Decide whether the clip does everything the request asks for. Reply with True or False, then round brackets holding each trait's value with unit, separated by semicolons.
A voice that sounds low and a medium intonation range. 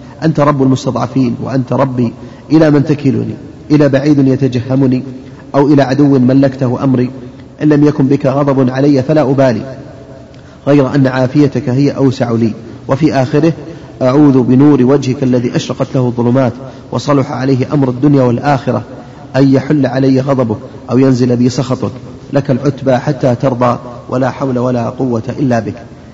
False (130 Hz; 1.8 semitones)